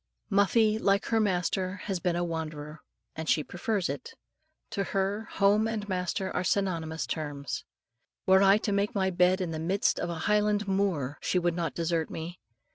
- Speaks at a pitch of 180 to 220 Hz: Yes, medium, 185 Hz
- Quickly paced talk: No, average, 180 wpm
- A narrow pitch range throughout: No, average, 3.4 semitones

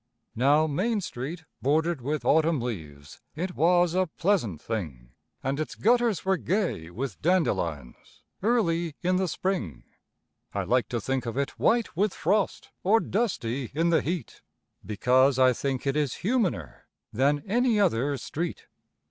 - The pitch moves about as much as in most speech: No, wide, 6.9 semitones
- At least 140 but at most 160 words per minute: Yes, average, 150 wpm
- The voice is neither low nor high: Yes, medium, 155 Hz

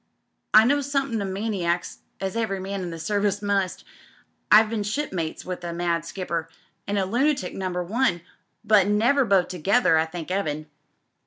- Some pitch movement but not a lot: Yes, average, 3.8 semitones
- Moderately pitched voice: No, high, 195 Hz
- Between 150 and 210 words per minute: Yes, average, 170 wpm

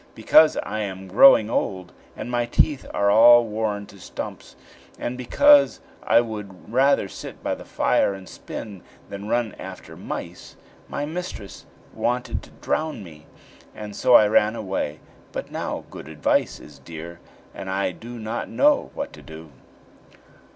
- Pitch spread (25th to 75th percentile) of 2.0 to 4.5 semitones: Yes, average, 4.2 semitones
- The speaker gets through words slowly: No, average, 155 wpm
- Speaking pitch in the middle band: No, low, 105 Hz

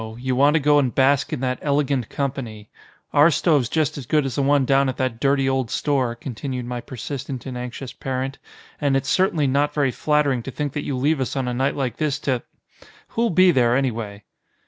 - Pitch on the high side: No, low, 135 Hz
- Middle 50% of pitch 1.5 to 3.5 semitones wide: Yes, narrow, 2.4 semitones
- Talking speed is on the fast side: Yes, fast, 215 wpm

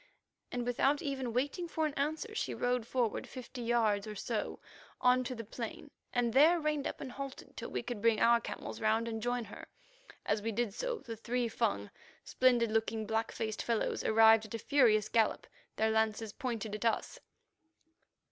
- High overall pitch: Yes, high, 235 Hz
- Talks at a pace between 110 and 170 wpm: No, average, 185 wpm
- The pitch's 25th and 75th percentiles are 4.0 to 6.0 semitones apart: No, average, 2.7 semitones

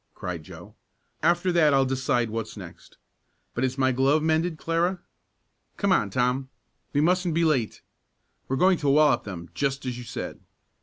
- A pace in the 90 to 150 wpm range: No, average, 165 wpm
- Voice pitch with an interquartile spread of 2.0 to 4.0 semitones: No, average, 4.9 semitones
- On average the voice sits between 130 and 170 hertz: Yes, low, 135 Hz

